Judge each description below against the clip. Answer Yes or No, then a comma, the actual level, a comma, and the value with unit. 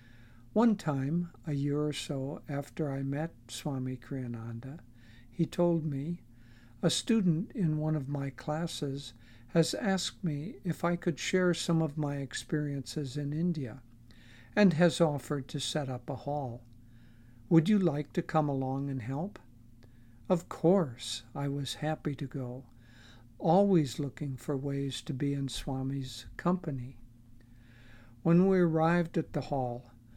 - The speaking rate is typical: Yes, average, 145 wpm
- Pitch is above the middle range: No, medium, 140 Hz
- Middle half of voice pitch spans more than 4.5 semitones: Yes, average, 5.3 semitones